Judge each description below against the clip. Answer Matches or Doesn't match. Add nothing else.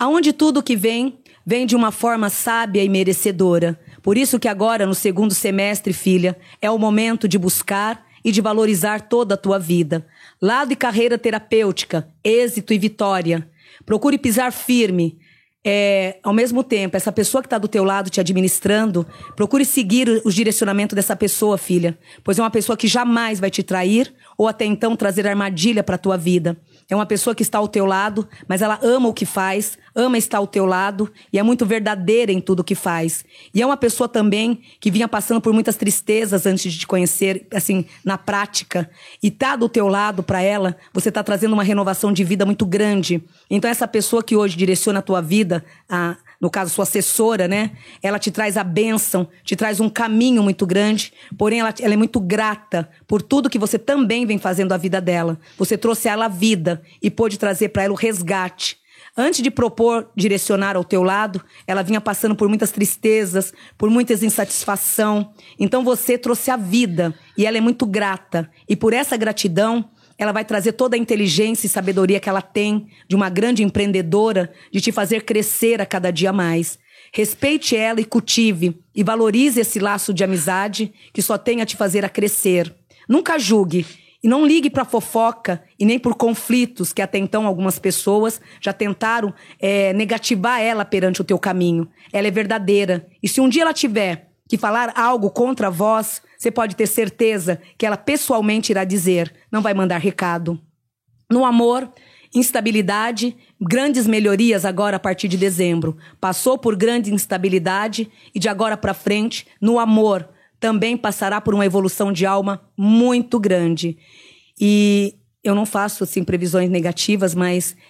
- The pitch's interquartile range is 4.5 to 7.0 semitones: Doesn't match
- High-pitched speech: Matches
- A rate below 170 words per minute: Doesn't match